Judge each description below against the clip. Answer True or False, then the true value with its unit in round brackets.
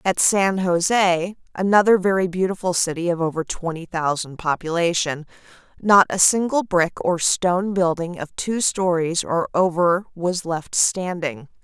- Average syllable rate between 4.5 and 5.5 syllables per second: False (4.3 syllables/s)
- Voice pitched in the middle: True (175 Hz)